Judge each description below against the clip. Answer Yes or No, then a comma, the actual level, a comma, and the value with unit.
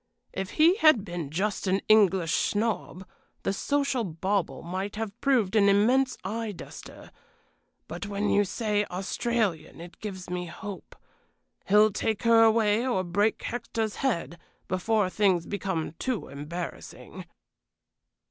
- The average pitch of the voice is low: No, high, 205 Hz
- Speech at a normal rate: No, slow, 130 wpm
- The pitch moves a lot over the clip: No, average, 3.5 semitones